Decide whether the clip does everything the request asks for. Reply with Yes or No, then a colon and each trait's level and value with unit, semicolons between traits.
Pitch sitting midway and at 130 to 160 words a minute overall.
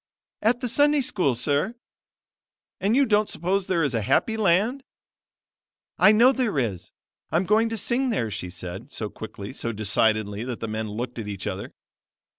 No: medium, 150 Hz; average, 175 wpm